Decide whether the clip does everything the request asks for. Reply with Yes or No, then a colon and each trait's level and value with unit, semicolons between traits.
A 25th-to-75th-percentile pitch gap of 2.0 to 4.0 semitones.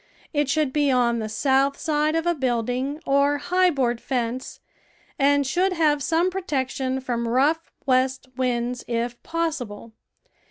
Yes: average, 3.5 semitones